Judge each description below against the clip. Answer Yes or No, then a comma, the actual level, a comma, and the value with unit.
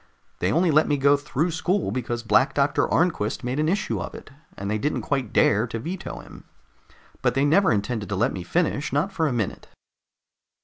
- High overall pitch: No, medium, 140 Hz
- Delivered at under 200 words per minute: No, fast, 205 wpm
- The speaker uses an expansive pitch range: Yes, wide, 5.8 semitones